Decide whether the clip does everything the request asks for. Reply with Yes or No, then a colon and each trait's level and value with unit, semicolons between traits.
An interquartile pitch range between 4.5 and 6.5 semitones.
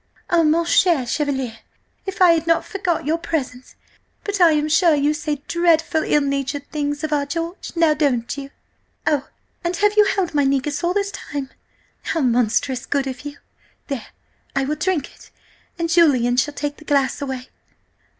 No: average, 3.3 semitones